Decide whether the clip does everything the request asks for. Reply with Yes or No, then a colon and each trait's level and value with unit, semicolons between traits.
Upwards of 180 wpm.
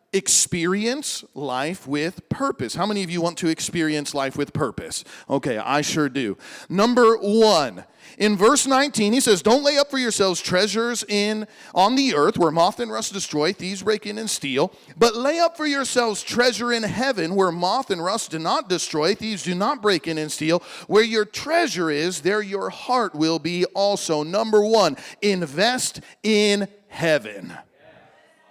No: average, 175 wpm